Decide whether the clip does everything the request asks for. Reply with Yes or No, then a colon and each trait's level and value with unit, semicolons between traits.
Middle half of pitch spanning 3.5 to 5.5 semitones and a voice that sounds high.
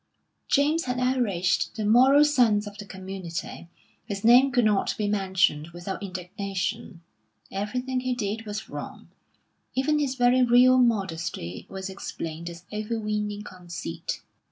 Yes: average, 4.8 semitones; high, 210 Hz